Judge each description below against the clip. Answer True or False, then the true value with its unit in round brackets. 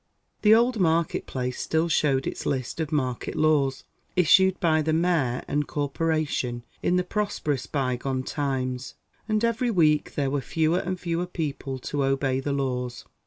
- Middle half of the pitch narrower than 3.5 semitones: False (4.3 semitones)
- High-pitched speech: False (150 Hz)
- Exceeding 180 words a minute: False (160 wpm)